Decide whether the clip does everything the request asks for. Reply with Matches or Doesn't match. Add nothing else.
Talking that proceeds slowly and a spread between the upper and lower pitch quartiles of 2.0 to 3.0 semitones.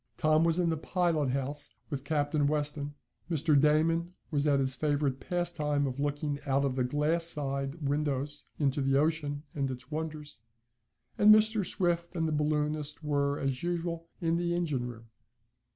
Doesn't match